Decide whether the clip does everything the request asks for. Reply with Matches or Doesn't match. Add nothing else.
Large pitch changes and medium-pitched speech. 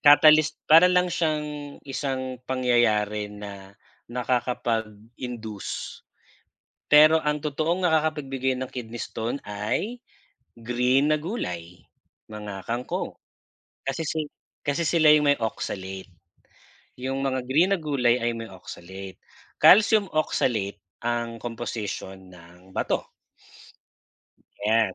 Doesn't match